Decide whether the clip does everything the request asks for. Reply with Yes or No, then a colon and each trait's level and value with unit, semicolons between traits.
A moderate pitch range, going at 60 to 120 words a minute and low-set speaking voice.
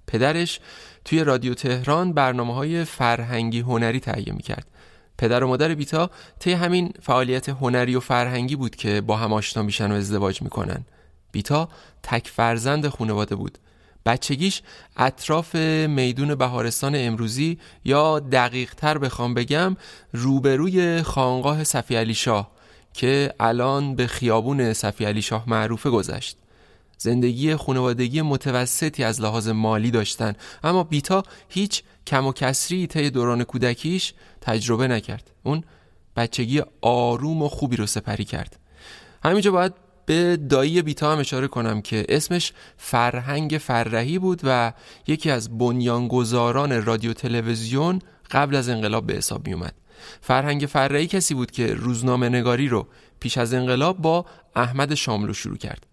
No: average, 4.4 semitones; average, 135 wpm; low, 125 Hz